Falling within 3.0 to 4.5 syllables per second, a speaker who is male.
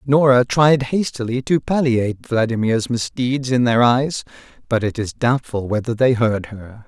Yes: 4.4 syllables/s; male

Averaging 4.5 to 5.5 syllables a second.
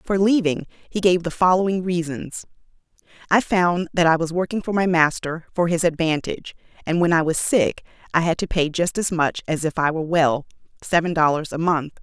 Yes: 5.4 syllables/s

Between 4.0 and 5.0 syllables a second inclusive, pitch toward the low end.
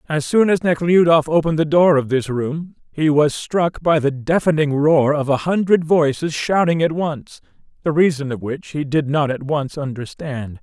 No: 4.7 syllables/s; medium, 150 Hz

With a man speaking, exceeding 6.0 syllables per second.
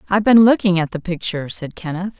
No: female; 6.5 syllables/s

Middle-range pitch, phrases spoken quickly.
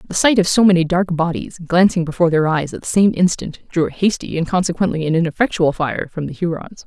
Yes: medium, 170 Hz; fast, 225 wpm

